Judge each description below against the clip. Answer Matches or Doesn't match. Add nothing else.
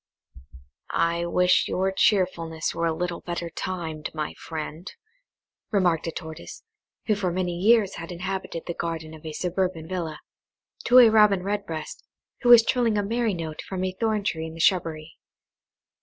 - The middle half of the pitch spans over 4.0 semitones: Doesn't match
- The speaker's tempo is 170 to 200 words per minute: Doesn't match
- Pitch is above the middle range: Doesn't match